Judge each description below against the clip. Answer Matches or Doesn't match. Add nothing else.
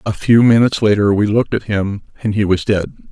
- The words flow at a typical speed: Doesn't match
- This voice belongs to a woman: Doesn't match